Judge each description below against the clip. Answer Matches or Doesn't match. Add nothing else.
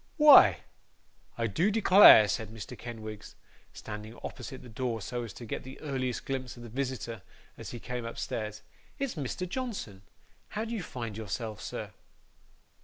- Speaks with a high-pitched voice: Doesn't match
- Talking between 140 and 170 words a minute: Matches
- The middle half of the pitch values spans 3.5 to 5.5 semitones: Matches